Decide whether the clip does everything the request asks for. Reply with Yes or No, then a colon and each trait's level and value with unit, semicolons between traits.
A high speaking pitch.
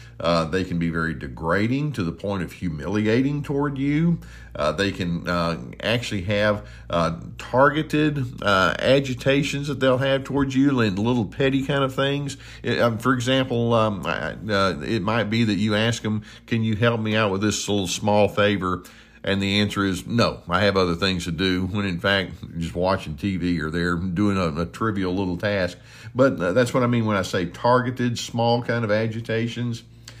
No: low, 110 Hz